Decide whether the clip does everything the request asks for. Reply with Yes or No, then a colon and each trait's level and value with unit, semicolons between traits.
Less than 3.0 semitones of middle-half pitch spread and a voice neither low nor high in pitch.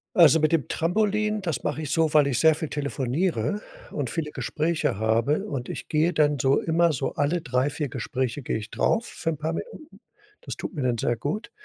No: average, 4.0 semitones; medium, 150 Hz